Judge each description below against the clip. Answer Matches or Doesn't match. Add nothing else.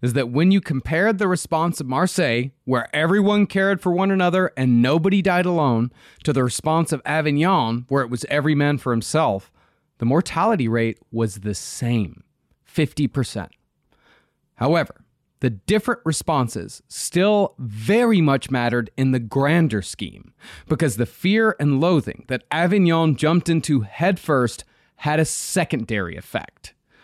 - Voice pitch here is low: Doesn't match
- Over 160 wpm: Doesn't match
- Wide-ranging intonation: Matches